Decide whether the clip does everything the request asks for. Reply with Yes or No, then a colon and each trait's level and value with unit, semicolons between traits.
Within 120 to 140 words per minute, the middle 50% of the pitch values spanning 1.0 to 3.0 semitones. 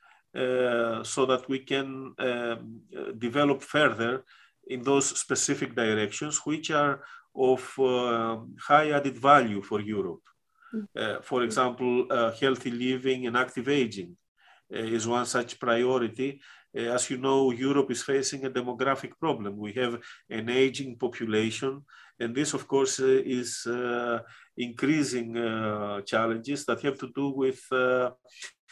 Yes: slow, 135 wpm; narrow, 2.6 semitones